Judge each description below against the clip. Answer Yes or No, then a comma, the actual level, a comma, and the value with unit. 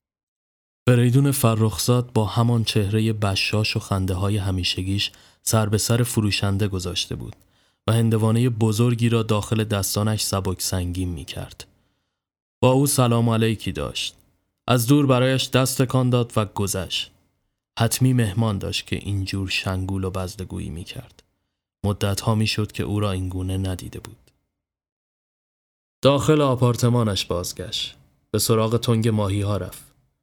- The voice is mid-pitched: No, low, 105 Hz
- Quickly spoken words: No, average, 135 wpm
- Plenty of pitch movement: No, average, 3.6 semitones